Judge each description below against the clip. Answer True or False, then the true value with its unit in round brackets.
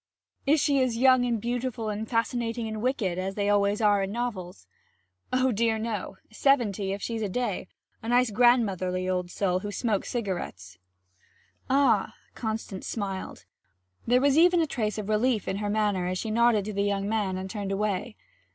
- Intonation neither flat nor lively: True (3.5 semitones)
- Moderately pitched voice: False (215 Hz)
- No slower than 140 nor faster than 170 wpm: False (180 wpm)